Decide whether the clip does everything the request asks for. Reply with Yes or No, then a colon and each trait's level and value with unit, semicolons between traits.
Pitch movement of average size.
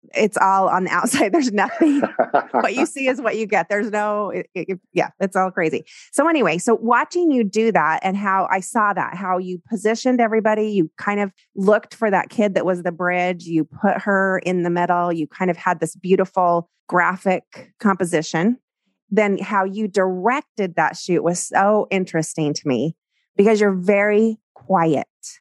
Yes: average, 3.3 semitones